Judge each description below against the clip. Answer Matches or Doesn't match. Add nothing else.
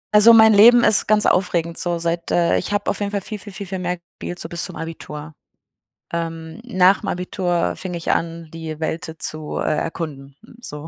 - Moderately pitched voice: Matches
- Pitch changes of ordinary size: Matches